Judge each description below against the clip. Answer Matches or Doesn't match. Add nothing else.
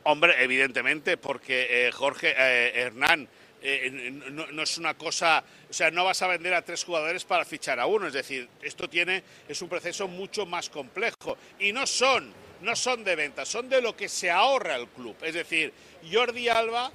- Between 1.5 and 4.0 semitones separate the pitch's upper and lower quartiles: Doesn't match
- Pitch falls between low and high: Matches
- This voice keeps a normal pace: Doesn't match